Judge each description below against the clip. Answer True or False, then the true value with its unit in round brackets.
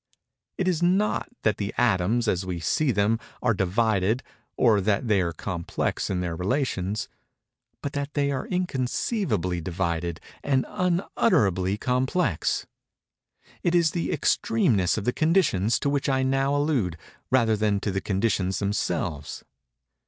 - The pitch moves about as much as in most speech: False (7.0 semitones)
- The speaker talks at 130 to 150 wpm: True (135 wpm)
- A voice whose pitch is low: True (110 Hz)